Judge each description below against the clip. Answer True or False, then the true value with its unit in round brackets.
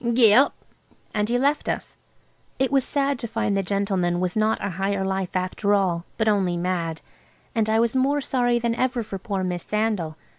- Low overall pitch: False (210 Hz)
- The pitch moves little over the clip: False (4.4 semitones)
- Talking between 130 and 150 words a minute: False (195 wpm)